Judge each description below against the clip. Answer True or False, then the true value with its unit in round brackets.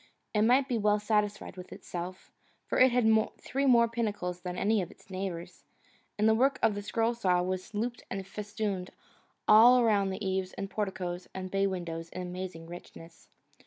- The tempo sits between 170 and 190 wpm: True (180 wpm)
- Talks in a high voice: True (200 Hz)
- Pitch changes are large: False (3.3 semitones)